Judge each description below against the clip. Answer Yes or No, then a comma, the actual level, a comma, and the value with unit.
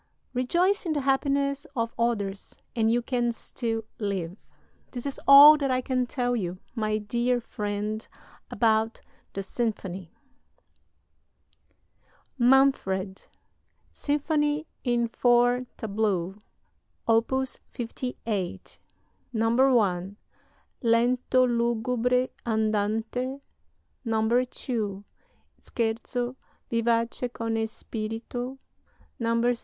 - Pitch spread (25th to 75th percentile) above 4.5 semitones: No, narrow, 2.5 semitones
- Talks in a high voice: Yes, high, 235 Hz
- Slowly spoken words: Yes, slow, 85 wpm